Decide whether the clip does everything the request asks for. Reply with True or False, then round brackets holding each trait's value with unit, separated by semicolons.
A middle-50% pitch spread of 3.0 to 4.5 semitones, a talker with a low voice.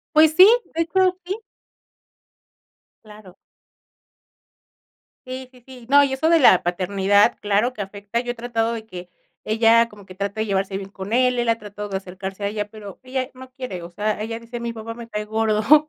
False (3.8 semitones; 220 Hz)